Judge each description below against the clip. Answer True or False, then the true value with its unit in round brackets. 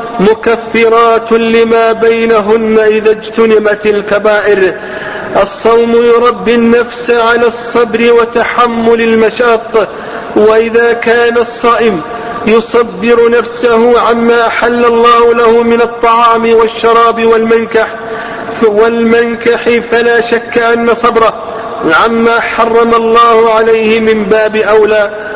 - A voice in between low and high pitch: False (230 Hz)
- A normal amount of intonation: False (0.8 semitones)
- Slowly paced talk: False (90 wpm)